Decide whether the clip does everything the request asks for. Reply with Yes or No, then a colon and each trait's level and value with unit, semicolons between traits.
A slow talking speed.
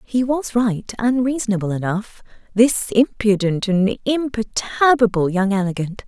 Yes: slow, 120 wpm